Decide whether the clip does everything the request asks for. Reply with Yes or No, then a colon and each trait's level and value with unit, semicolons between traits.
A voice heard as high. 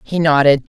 No: medium, 150 Hz